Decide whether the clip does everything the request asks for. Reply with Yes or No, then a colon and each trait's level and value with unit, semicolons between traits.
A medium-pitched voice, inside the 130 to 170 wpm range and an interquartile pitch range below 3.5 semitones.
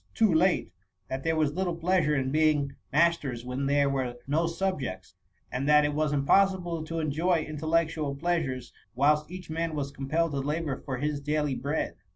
No: medium, 150 Hz; average, 180 wpm; average, 3.1 semitones